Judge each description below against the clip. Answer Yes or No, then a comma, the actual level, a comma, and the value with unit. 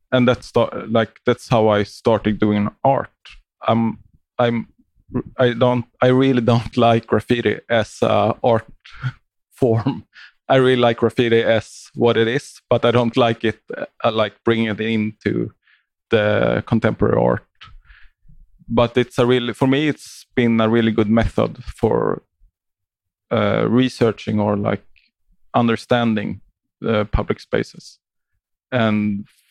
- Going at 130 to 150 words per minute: Yes, average, 140 wpm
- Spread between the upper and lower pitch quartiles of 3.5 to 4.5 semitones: No, narrow, 2.6 semitones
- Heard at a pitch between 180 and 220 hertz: No, low, 115 Hz